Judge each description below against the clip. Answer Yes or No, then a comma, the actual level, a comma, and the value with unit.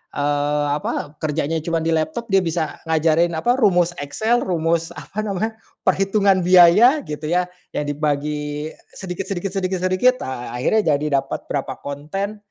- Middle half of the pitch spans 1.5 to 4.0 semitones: No, average, 4.6 semitones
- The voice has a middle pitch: Yes, medium, 170 Hz